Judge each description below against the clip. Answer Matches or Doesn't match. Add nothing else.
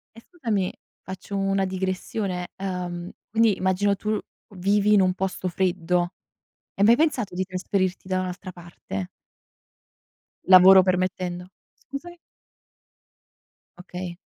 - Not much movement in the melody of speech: Matches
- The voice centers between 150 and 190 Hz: Matches